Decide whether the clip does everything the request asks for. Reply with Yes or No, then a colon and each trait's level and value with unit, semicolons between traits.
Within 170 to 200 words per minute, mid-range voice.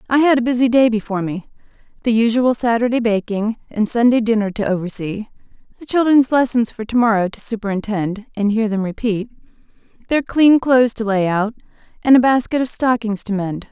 No: average, 180 wpm; high, 225 Hz